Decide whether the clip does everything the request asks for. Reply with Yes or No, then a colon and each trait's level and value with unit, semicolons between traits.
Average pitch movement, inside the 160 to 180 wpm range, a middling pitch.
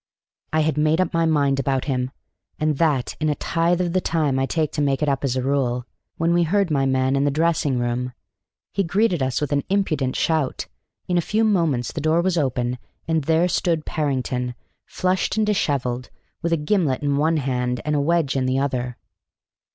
No: average, 4.1 semitones; fast, 205 wpm; medium, 150 Hz